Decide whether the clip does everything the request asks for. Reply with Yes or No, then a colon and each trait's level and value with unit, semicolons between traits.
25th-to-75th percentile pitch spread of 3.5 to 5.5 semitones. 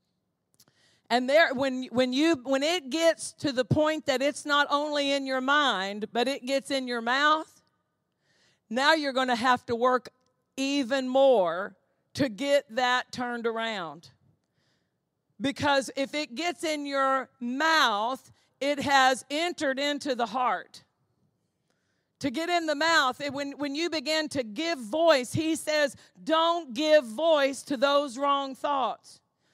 No: average, 3.0 semitones